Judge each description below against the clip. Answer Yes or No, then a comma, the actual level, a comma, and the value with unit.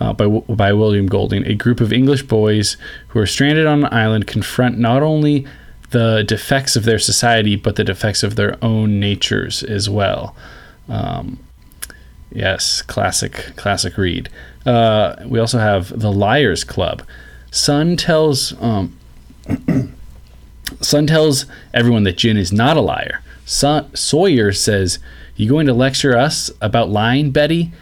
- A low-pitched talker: Yes, low, 110 Hz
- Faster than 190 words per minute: No, average, 145 wpm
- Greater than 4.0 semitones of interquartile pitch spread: Yes, average, 4.7 semitones